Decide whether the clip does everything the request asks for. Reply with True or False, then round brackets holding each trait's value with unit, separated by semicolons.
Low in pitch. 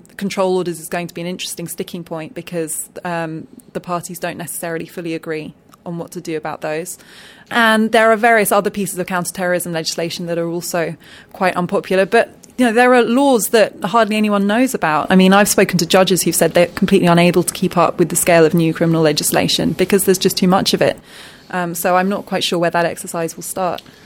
False (180 Hz)